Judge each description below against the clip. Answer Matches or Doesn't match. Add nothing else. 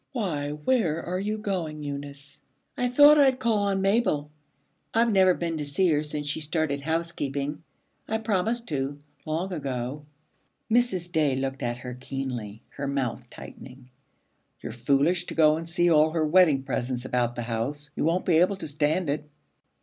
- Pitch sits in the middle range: Matches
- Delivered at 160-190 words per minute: Matches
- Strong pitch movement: Doesn't match